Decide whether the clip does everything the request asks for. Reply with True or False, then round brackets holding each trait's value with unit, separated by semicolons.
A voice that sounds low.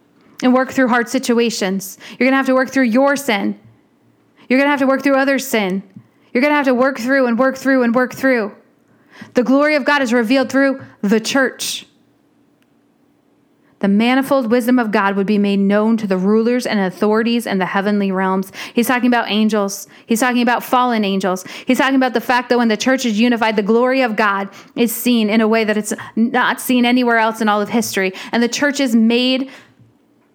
False (240 Hz)